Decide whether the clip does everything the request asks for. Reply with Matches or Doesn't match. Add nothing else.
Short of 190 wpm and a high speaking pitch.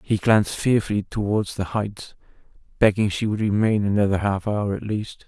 Doesn't match